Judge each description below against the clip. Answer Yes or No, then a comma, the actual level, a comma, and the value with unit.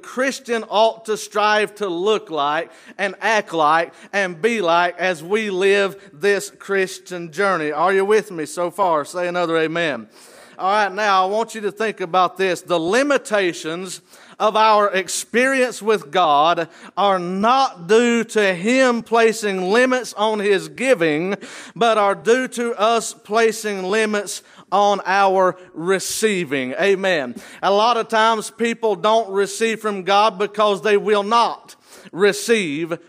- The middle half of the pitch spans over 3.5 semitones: No, average, 3.1 semitones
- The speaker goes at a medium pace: Yes, average, 145 wpm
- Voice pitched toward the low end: No, high, 205 Hz